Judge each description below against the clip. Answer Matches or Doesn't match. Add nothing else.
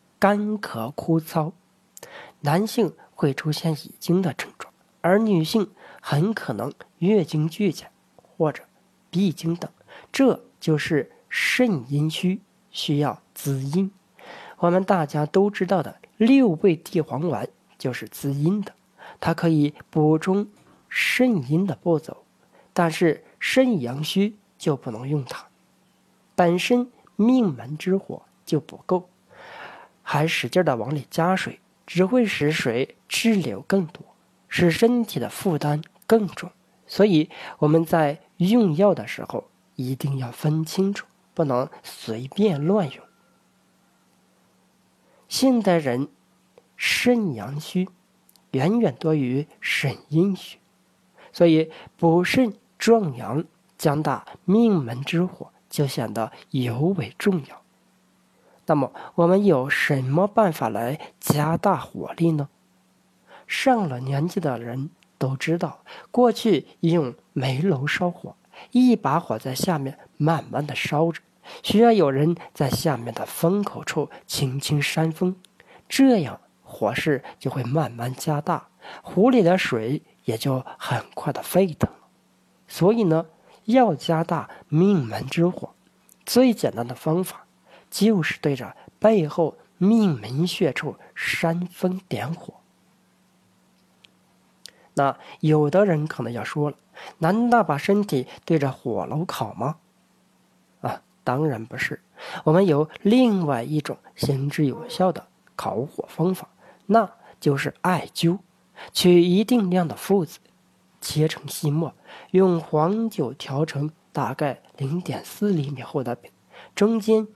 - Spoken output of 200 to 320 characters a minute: Doesn't match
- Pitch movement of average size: Matches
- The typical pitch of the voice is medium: Matches